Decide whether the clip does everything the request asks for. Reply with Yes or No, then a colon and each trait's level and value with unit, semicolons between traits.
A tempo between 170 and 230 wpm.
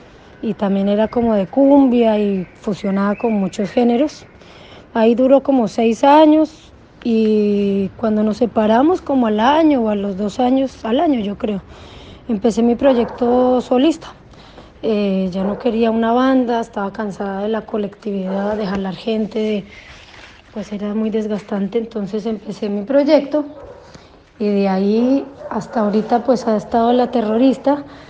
No: average, 145 wpm